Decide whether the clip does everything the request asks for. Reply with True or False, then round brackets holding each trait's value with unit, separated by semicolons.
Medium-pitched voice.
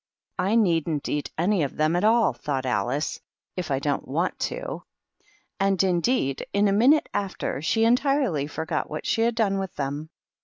True (180 Hz)